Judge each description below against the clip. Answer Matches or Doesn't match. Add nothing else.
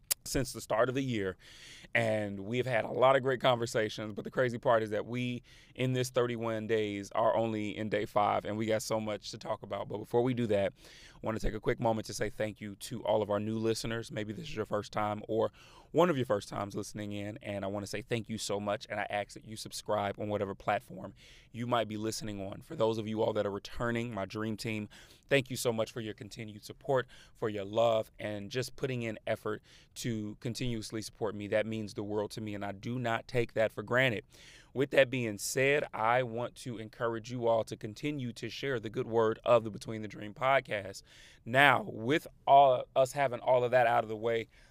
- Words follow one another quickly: Matches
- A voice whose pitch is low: Matches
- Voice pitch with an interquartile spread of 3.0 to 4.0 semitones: Doesn't match